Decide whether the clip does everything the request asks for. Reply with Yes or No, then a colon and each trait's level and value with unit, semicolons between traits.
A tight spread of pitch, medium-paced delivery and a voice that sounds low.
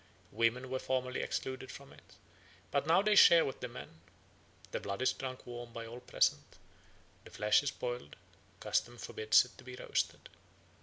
Yes: narrow, 2.0 semitones; average, 170 wpm; low, 125 Hz